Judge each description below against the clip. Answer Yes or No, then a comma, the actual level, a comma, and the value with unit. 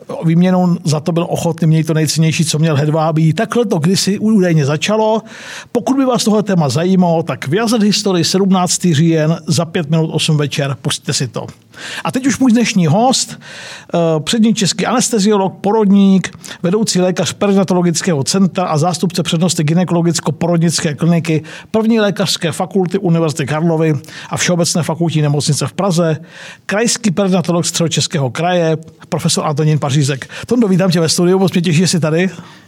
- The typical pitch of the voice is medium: Yes, medium, 175 Hz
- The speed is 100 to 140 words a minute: No, average, 155 wpm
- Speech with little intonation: No, average, 3.4 semitones